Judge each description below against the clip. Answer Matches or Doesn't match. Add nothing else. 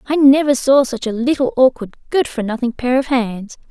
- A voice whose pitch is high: Matches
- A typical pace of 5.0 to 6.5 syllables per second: Matches